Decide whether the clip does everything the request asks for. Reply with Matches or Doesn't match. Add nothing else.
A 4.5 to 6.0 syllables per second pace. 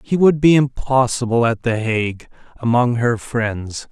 Doesn't match